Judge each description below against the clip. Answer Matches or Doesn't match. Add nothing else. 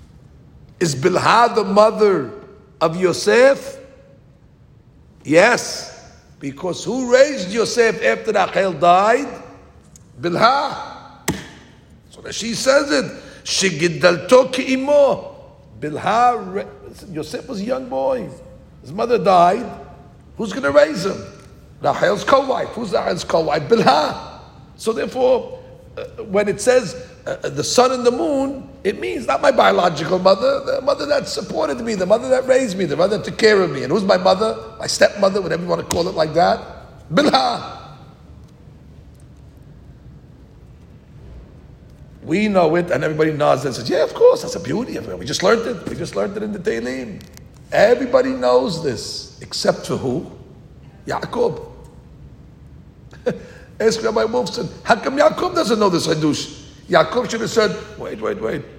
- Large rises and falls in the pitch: Matches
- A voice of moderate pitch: Doesn't match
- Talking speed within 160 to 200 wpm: Doesn't match